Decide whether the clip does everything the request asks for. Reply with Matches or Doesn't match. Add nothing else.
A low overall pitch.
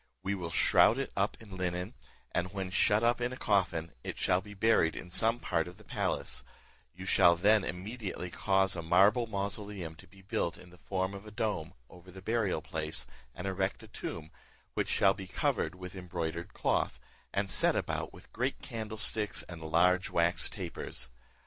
Matches